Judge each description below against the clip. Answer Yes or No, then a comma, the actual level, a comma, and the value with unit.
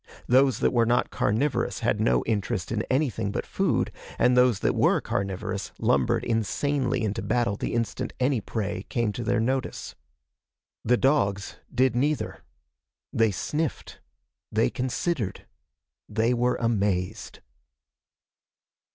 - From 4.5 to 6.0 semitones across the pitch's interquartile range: No, average, 3.7 semitones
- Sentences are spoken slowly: Yes, slow, 125 wpm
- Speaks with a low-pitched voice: Yes, low, 115 Hz